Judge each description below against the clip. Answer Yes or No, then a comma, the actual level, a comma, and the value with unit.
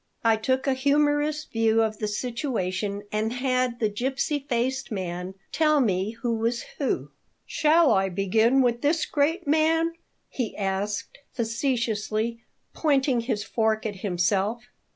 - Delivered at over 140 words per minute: No, slow, 135 wpm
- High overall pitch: Yes, high, 235 Hz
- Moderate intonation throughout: Yes, average, 4.6 semitones